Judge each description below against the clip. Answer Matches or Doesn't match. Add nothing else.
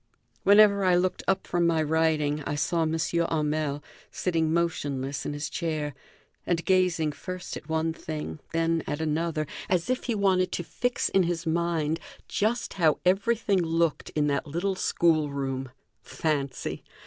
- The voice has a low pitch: Doesn't match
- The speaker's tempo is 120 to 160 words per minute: Matches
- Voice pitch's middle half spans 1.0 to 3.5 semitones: Matches